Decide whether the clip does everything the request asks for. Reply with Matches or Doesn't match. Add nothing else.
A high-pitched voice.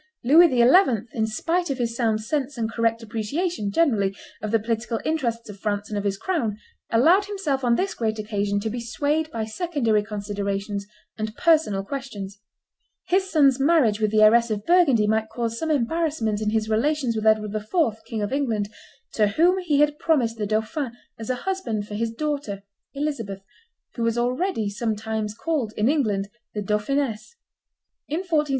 Matches